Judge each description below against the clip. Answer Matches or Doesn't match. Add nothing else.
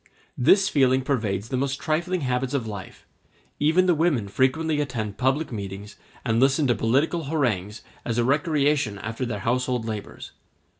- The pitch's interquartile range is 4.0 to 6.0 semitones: Matches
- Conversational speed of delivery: Matches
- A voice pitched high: Doesn't match